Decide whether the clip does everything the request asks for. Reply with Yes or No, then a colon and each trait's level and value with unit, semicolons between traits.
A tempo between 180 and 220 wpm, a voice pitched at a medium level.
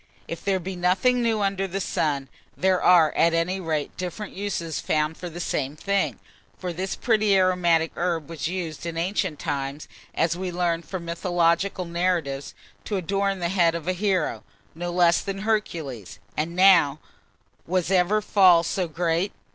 No: average, 165 wpm; medium, 175 Hz